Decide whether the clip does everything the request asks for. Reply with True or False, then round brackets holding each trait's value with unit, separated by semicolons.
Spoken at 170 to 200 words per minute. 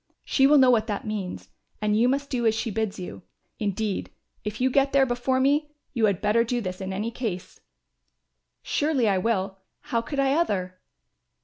True (190 wpm)